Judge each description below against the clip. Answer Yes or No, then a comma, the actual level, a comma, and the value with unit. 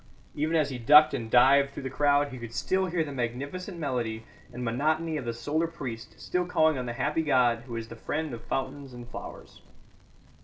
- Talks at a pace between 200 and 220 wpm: Yes, fast, 205 wpm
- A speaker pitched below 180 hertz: Yes, low, 135 Hz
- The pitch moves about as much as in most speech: Yes, average, 4.5 semitones